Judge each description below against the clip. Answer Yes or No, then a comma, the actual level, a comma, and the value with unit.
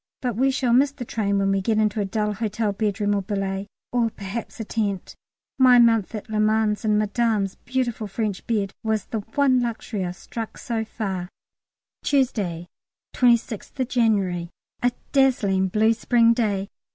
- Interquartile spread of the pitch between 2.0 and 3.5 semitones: Yes, average, 3.0 semitones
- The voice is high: Yes, high, 220 Hz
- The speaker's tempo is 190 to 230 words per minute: No, average, 165 wpm